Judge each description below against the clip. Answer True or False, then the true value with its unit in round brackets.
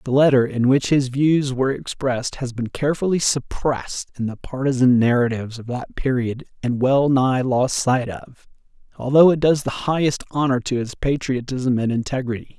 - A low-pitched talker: True (130 Hz)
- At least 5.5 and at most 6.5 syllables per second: False (5.1 syllables/s)